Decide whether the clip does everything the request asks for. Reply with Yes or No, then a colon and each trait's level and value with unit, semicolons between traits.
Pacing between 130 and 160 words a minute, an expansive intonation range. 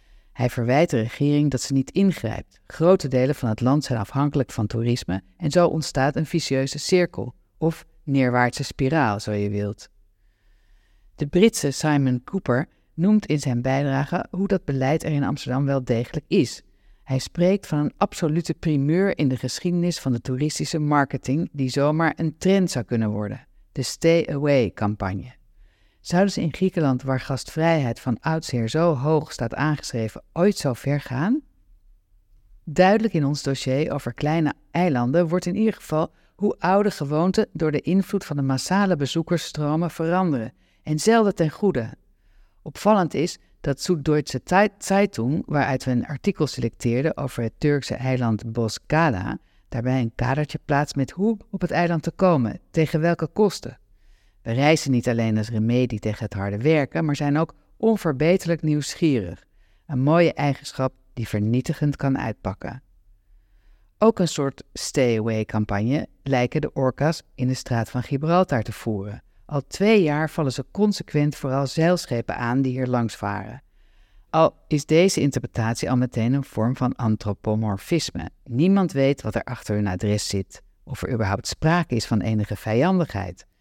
Yes: average, 155 wpm; wide, 6.0 semitones